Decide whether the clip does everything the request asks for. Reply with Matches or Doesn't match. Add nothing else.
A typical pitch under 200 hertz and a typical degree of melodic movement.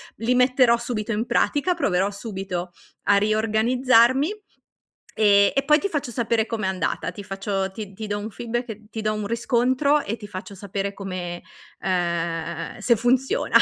Doesn't match